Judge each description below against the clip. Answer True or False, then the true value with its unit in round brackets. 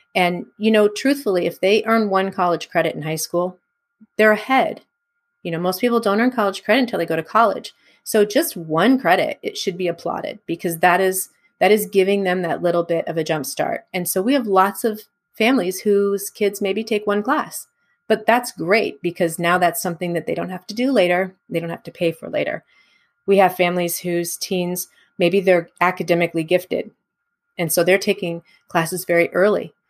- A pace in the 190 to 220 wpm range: True (200 wpm)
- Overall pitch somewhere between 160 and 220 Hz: True (190 Hz)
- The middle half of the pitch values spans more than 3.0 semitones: True (3.8 semitones)